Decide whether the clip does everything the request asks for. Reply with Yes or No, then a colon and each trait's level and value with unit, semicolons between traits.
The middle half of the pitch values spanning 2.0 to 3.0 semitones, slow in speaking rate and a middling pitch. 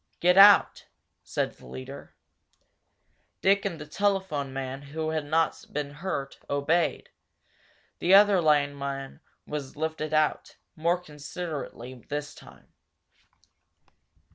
No: average, 3.7 semitones; slow, 110 wpm; medium, 150 Hz